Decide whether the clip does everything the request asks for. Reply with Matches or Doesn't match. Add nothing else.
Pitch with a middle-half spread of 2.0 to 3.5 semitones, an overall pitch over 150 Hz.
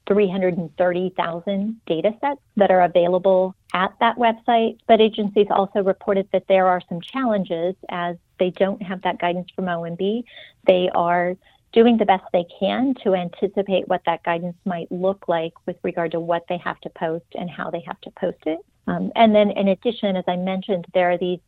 Matches